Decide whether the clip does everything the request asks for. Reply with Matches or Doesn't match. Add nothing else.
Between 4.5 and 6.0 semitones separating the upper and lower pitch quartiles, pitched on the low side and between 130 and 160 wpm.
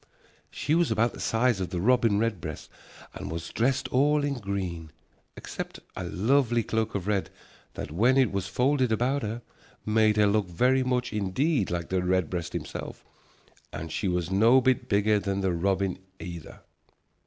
Doesn't match